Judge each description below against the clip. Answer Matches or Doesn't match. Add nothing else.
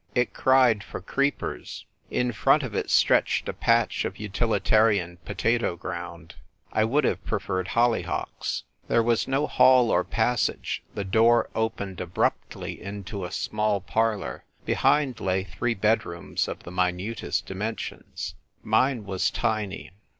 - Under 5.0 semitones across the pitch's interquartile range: Matches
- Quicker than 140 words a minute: Doesn't match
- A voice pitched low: Matches